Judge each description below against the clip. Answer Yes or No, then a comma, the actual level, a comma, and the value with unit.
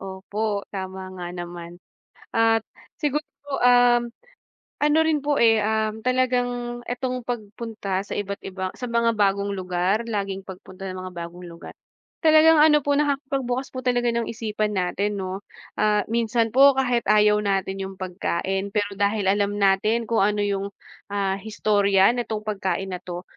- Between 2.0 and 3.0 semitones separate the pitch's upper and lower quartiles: No, average, 3.9 semitones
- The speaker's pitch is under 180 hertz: No, high, 210 Hz